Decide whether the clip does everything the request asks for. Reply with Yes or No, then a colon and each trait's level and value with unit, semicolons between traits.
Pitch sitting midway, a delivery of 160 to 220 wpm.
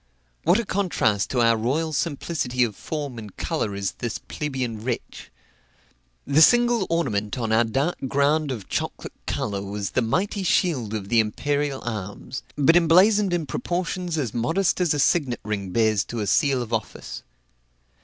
No: low, 130 Hz; average, 165 wpm